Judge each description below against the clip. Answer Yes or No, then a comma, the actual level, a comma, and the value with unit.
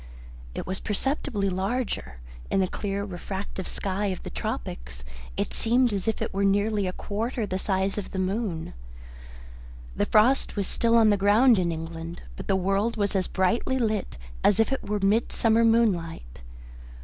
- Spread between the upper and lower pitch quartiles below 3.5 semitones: Yes, average, 3.1 semitones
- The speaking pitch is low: No, high, 200 Hz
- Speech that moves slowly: No, average, 170 wpm